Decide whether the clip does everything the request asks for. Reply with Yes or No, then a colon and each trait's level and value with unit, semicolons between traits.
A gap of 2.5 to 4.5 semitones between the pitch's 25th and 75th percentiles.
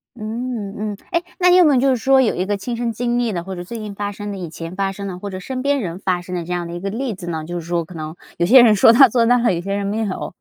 No: average, 5.1 semitones